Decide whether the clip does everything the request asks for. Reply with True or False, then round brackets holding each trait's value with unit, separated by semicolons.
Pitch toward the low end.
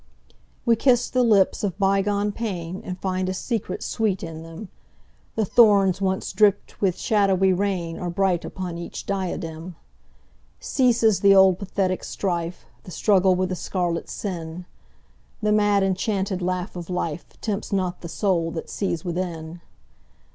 False (190 Hz)